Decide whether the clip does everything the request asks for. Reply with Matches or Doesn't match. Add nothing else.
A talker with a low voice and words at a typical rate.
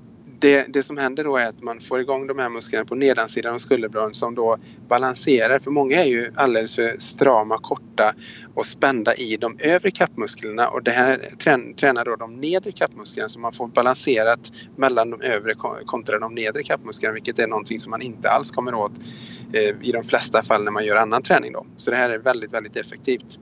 Doesn't match